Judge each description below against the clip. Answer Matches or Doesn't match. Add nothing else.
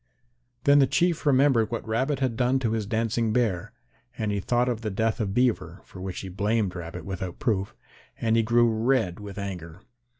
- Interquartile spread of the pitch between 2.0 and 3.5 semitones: Doesn't match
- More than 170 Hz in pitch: Doesn't match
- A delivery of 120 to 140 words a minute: Doesn't match